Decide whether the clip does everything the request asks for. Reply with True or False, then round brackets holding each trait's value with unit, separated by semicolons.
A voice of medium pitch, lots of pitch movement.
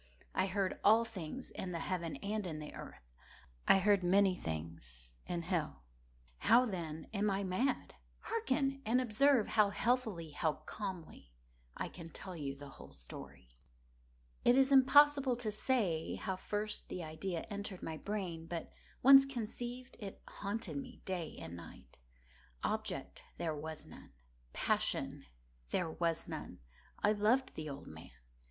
False (195 Hz; 6.4 semitones)